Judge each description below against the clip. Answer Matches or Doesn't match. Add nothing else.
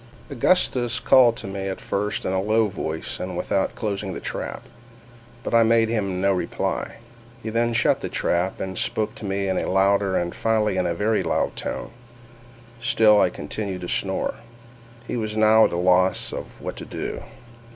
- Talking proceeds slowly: Doesn't match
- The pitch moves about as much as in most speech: Matches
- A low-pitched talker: Matches